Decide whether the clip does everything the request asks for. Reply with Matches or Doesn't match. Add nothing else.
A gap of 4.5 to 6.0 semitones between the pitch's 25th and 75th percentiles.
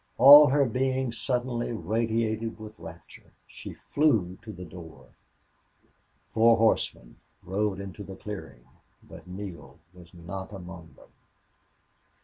Matches